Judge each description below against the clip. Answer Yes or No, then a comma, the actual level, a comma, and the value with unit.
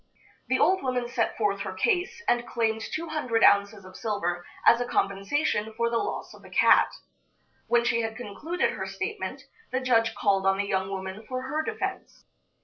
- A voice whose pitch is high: Yes, high, 230 Hz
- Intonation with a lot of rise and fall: No, average, 4.4 semitones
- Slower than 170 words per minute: No, average, 185 wpm